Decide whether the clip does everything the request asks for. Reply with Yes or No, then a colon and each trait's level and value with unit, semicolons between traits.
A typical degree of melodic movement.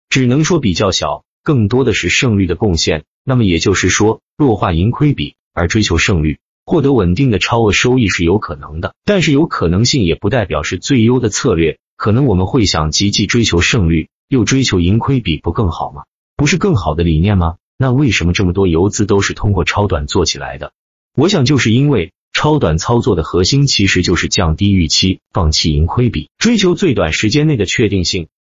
No: wide, 7.0 semitones